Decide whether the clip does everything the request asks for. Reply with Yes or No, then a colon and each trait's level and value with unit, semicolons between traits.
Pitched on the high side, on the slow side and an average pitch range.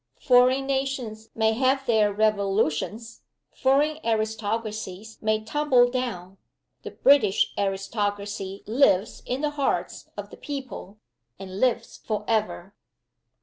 Yes: high, 220 Hz; slow, 105 wpm; average, 4.2 semitones